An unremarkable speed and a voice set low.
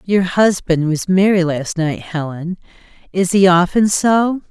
No: average, 145 wpm; medium, 180 Hz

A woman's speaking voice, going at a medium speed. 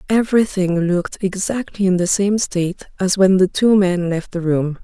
Yes: female; average, 185 wpm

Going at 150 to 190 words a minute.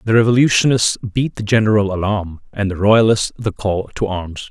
Yes: average, 175 wpm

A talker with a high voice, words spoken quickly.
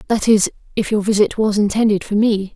Yes: high, 210 Hz; fast, 210 wpm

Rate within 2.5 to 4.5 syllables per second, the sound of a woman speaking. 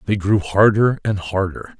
No: 4.4 syllables/s; male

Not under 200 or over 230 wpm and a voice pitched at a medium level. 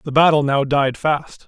Yes: fast, 205 wpm; medium, 145 Hz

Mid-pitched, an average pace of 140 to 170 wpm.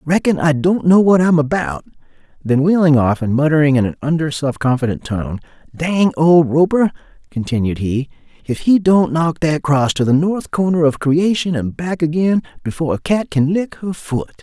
No: medium, 155 Hz; average, 185 wpm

